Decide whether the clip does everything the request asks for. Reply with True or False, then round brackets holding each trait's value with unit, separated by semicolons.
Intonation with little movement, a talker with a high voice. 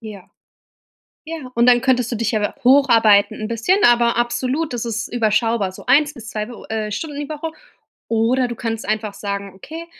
False (3.2 semitones; 235 Hz)